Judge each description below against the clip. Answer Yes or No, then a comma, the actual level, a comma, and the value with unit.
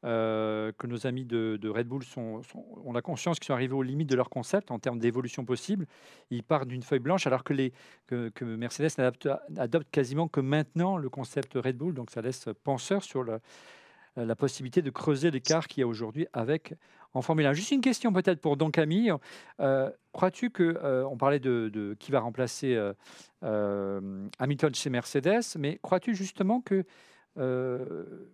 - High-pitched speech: No, low, 135 Hz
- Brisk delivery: No, average, 195 wpm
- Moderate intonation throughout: Yes, average, 4.9 semitones